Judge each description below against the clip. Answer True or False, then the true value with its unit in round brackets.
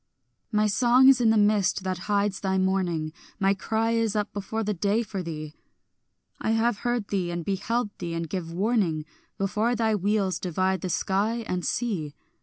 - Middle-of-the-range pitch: False (200 Hz)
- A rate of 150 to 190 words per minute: True (180 wpm)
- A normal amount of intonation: True (3.2 semitones)